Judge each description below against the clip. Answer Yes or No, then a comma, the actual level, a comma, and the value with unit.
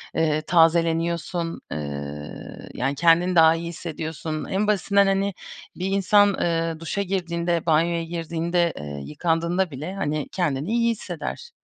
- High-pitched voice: No, medium, 170 Hz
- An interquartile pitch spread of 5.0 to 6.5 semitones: No, narrow, 2.4 semitones